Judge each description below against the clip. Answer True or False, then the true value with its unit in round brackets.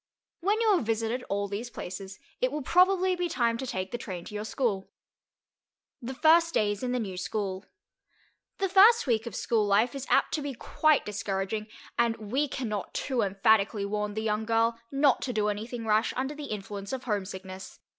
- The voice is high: True (225 Hz)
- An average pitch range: True (4.6 semitones)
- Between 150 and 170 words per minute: False (195 wpm)